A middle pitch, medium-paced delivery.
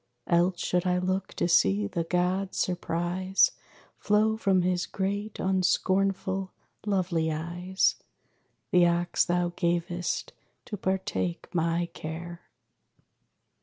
No: medium, 180 Hz; slow, 105 wpm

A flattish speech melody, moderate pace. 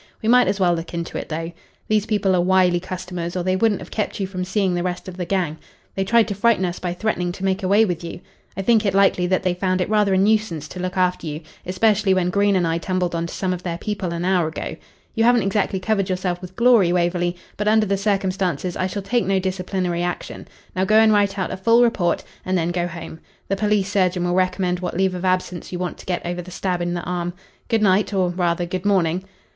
No: narrow, 2.0 semitones; fast, 250 wpm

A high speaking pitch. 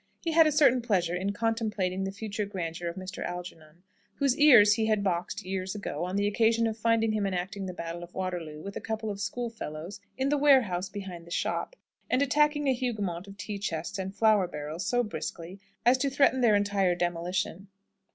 Yes: high, 200 Hz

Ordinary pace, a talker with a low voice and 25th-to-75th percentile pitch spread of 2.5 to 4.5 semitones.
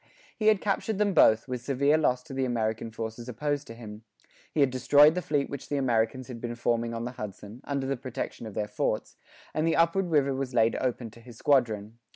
No: fast, 220 wpm; low, 125 Hz; average, 4.0 semitones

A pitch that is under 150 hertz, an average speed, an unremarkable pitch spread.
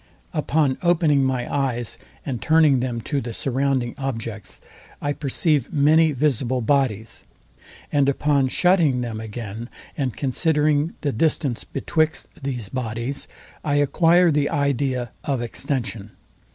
No: low, 135 Hz; slow, 125 wpm; average, 3.6 semitones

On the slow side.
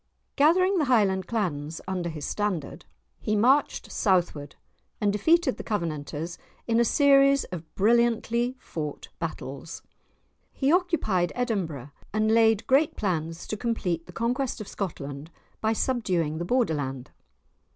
Yes: slow, 130 wpm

